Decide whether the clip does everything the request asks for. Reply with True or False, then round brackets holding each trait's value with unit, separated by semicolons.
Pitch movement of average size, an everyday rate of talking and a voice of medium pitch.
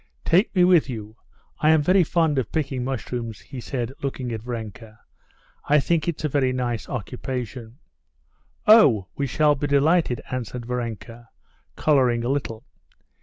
False (4.0 semitones; 150 wpm; 130 Hz)